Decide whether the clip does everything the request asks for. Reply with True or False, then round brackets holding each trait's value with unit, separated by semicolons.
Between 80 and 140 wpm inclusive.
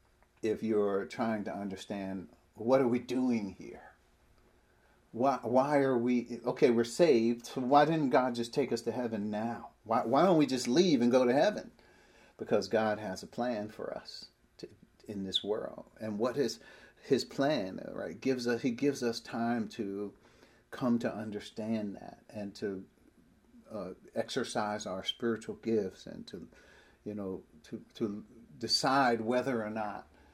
False (160 wpm)